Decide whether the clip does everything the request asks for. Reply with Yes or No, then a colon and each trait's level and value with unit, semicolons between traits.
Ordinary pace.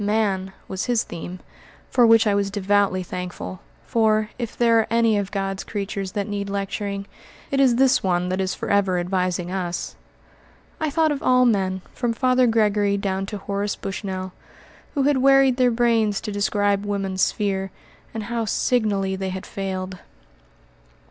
Yes: average, 160 wpm